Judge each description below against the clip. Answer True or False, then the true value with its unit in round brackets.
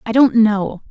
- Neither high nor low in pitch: False (220 Hz)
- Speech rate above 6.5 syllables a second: False (4.1 syllables/s)